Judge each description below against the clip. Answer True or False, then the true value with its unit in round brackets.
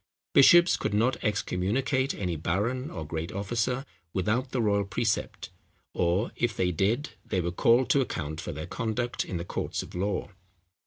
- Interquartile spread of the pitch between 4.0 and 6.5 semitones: True (5.6 semitones)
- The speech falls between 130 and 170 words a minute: True (165 wpm)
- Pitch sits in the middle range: False (105 Hz)